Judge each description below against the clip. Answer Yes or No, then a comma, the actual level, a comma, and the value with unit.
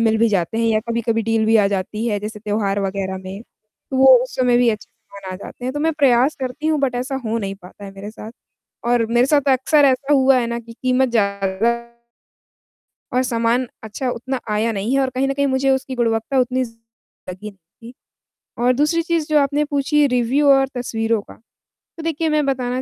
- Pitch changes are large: No, average, 3.8 semitones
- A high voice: Yes, high, 245 Hz